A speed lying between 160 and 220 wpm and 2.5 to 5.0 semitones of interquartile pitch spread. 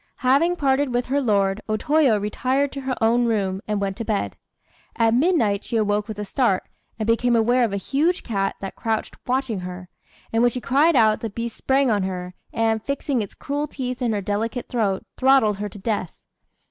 Yes: fast, 205 wpm; average, 4.2 semitones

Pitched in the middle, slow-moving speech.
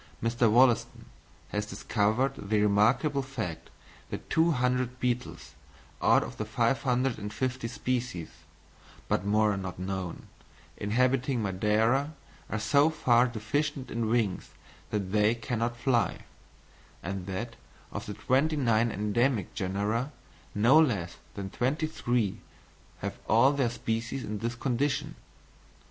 No: low, 115 Hz; slow, 120 wpm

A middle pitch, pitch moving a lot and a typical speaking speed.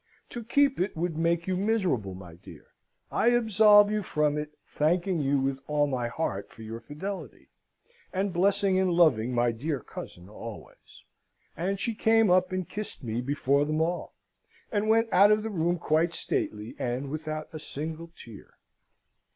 Yes: medium, 165 Hz; wide, 6.3 semitones; average, 165 wpm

